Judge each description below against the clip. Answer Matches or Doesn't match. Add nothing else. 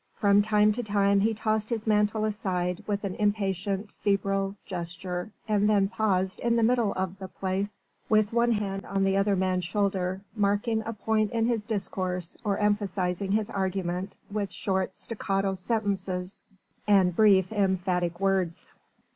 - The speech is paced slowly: Doesn't match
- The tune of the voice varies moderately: Doesn't match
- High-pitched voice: Matches